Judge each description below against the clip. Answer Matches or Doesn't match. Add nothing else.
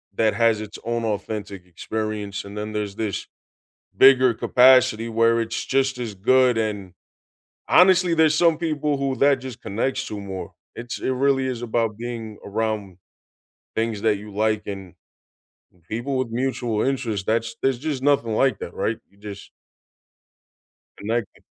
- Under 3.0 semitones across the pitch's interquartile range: Doesn't match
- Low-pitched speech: Matches